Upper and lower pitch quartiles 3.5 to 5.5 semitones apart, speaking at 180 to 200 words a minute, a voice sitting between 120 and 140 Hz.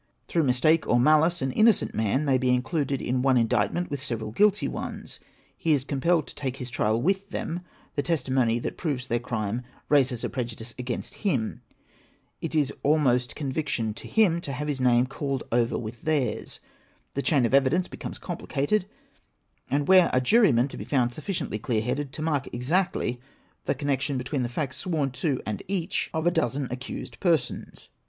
Yes: average, 4.2 semitones; average, 185 wpm; low, 135 Hz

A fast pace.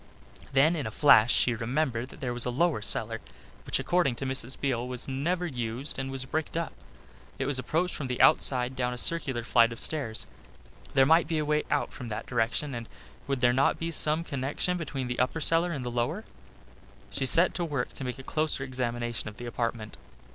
Yes: fast, 210 wpm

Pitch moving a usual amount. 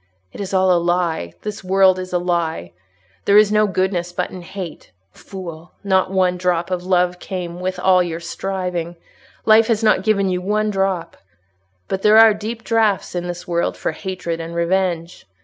No: narrow, 2.1 semitones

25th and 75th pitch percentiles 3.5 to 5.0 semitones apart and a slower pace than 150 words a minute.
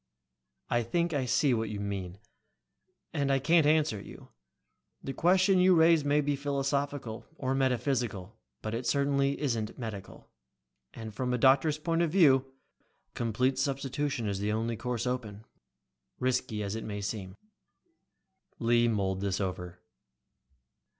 Yes: average, 4.7 semitones; average, 140 wpm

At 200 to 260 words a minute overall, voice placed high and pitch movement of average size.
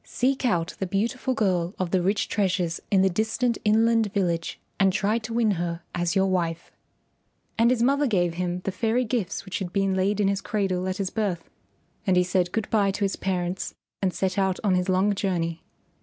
Yes: fast, 205 wpm; high, 195 Hz; average, 3.1 semitones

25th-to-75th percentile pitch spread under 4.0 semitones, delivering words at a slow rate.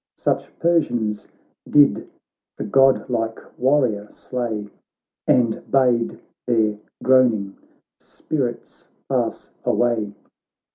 Yes: average, 3.2 semitones; slow, 80 wpm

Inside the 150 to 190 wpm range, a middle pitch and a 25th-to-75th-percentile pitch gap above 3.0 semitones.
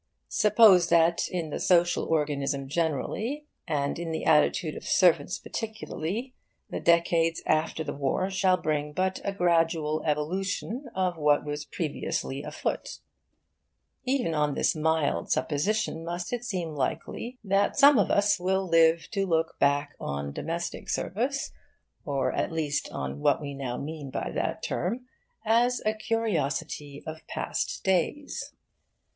No: average, 140 wpm; medium, 165 Hz; average, 4.6 semitones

